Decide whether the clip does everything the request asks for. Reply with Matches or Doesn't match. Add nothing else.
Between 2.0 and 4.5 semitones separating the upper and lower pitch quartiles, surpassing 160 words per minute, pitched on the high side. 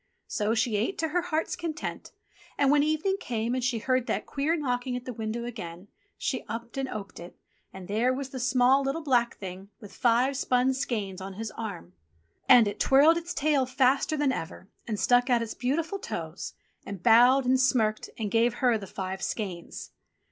Matches